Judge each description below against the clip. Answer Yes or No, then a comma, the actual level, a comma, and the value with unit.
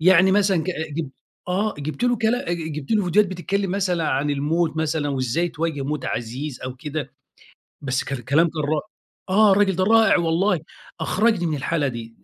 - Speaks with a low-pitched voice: No, medium, 165 Hz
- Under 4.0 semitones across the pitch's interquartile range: No, average, 4.8 semitones